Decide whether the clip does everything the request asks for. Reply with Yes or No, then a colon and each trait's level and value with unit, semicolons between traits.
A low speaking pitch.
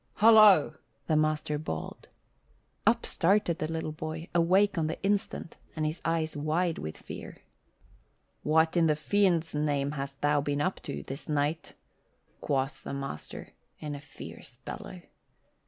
No: medium, 155 Hz